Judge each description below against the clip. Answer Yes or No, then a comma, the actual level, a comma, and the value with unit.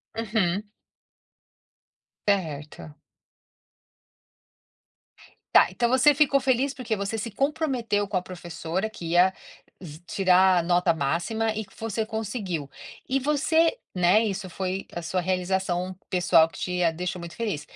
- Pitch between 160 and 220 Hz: Yes, high, 190 Hz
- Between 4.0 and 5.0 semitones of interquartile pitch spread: Yes, average, 4.3 semitones